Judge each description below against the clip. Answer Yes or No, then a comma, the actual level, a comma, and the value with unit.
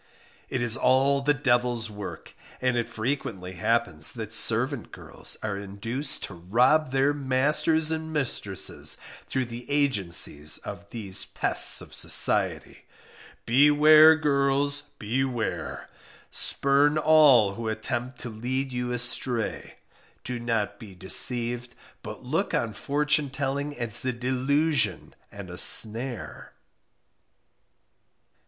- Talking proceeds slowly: Yes, slow, 115 wpm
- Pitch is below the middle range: Yes, low, 125 Hz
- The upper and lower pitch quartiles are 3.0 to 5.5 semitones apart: Yes, average, 3.9 semitones